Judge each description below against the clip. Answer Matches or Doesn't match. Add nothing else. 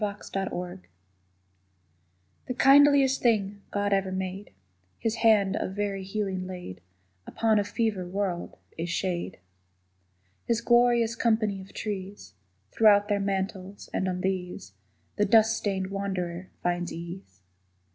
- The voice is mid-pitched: Doesn't match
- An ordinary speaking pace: Doesn't match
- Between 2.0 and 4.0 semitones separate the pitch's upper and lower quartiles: Matches